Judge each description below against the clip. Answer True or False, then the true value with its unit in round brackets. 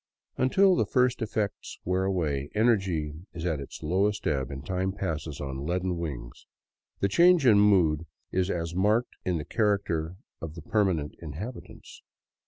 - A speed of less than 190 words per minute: True (160 wpm)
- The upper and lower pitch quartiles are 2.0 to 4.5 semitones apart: False (5.1 semitones)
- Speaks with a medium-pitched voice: False (90 Hz)